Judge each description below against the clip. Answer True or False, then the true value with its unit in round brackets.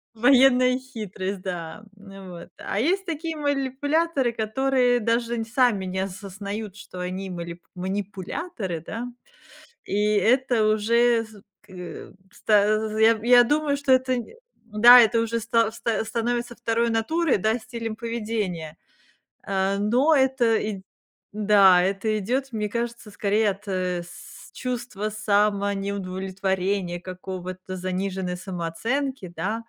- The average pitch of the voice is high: True (215 Hz)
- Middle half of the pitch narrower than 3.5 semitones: False (4.1 semitones)